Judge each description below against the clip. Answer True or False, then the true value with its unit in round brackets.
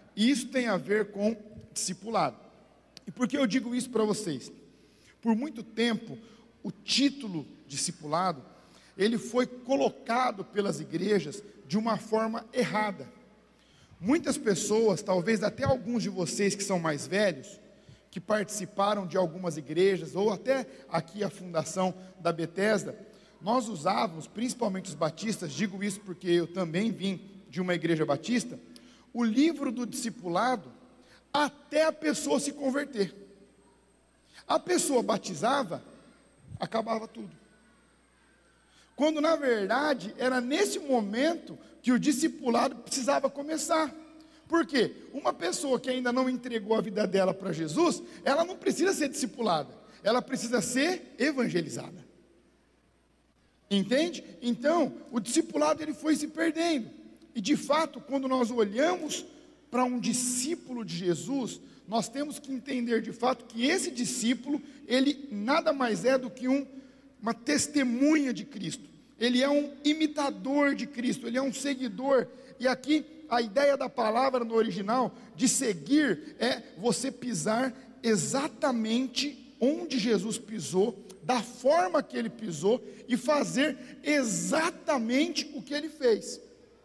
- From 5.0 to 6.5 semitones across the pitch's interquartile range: True (5.3 semitones)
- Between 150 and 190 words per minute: False (135 wpm)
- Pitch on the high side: True (245 Hz)